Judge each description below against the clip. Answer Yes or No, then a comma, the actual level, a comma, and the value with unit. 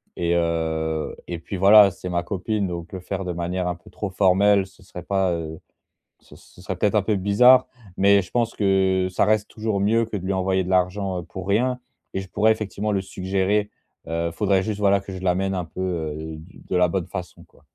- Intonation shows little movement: Yes, narrow, 2.3 semitones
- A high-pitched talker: No, very low, 95 Hz